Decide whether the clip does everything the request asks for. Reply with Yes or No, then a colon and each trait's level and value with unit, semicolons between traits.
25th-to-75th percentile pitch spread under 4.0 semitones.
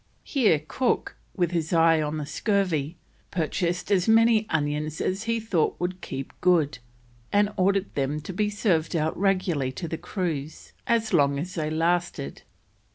No: average, 4.5 semitones